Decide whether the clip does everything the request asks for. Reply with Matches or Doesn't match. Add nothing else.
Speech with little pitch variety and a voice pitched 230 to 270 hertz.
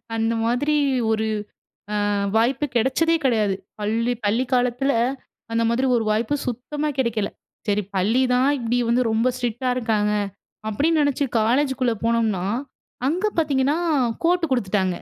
Doesn't match